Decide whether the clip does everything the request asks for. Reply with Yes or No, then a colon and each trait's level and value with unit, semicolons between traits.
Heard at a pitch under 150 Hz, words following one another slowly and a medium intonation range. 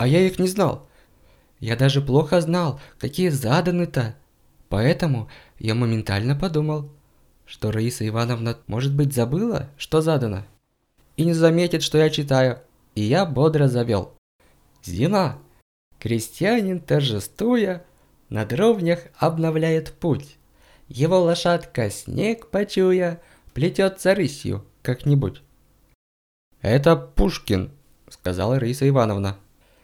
No: medium, 140 Hz; slow, 105 wpm; wide, 6.7 semitones